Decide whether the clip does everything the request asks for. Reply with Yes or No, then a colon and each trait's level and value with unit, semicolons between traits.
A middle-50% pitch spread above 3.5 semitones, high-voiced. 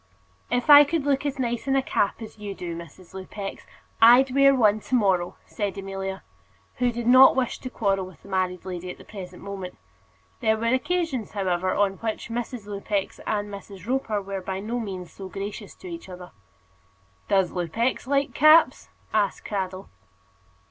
Yes: average, 4.6 semitones; high, 205 Hz